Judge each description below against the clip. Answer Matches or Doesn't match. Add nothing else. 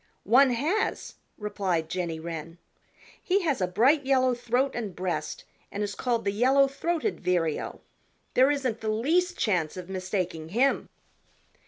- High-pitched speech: Matches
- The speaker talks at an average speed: Matches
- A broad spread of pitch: Matches